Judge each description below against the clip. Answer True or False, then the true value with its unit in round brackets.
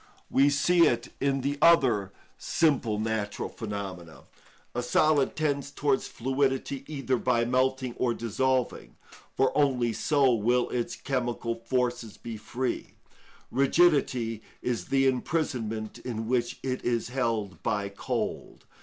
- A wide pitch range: False (2.9 semitones)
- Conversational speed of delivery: False (125 wpm)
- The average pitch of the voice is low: True (125 Hz)